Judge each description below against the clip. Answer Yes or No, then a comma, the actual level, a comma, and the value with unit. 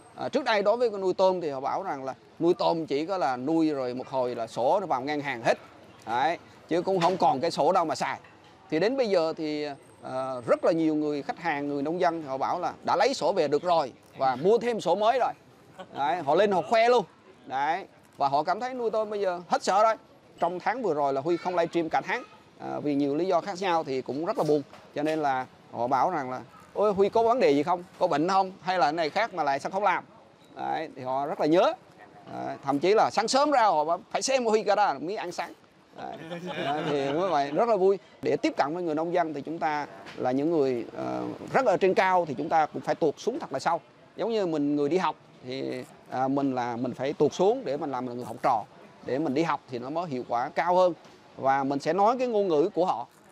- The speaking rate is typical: No, fast, 265 wpm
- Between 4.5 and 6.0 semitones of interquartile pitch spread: Yes, wide, 5.6 semitones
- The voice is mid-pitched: Yes, medium, 160 Hz